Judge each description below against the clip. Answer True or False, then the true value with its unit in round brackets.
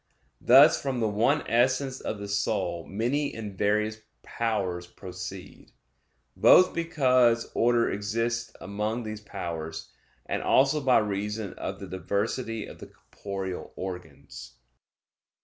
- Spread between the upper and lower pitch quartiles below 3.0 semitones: False (3.6 semitones)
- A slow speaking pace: True (120 wpm)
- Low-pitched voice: True (110 Hz)